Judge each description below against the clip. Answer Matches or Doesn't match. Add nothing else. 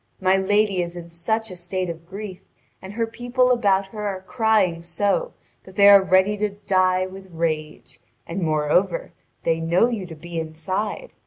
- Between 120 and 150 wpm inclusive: Doesn't match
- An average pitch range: Matches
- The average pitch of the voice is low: Doesn't match